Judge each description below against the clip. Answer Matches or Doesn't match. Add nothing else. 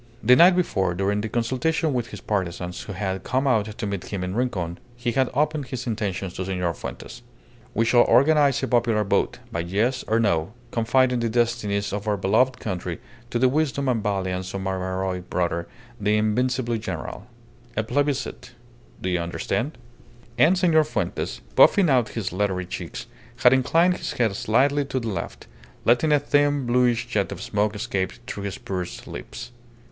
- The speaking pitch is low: Matches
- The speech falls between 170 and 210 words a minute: Matches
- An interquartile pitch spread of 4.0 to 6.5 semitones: Matches